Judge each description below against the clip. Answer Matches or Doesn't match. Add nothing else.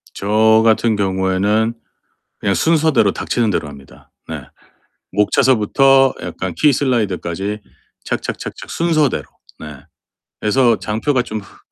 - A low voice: Matches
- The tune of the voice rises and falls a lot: Doesn't match